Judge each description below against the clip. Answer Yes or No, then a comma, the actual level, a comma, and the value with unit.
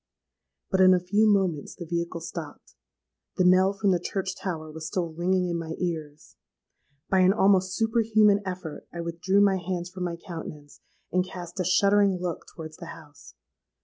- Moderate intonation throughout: No, narrow, 2.3 semitones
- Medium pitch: Yes, medium, 180 Hz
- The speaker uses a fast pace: No, average, 175 wpm